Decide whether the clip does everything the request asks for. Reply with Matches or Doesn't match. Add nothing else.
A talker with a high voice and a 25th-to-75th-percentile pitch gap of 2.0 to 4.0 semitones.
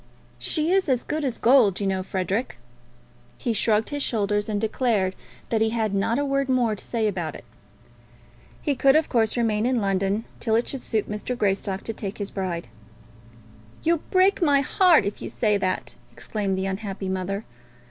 Doesn't match